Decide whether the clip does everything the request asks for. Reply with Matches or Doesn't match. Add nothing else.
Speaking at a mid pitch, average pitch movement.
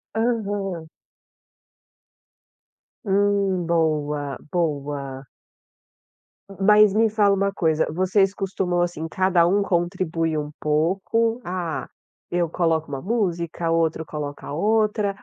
Matches